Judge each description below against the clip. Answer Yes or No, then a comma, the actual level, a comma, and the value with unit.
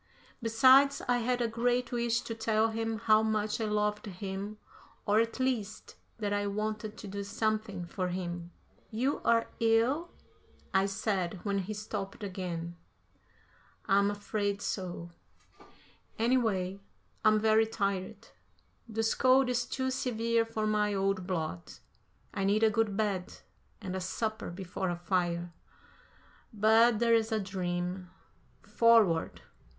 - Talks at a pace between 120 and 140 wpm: Yes, slow, 135 wpm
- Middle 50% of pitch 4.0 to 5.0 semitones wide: No, average, 2.9 semitones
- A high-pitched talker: Yes, high, 215 Hz